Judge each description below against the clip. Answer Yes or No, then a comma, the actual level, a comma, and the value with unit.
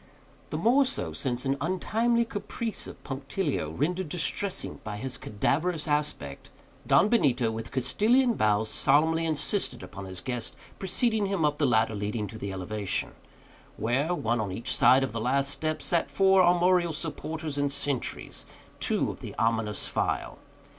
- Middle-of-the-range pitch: Yes, medium, 145 Hz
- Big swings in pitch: Yes, wide, 7.8 semitones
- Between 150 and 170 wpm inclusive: Yes, average, 160 wpm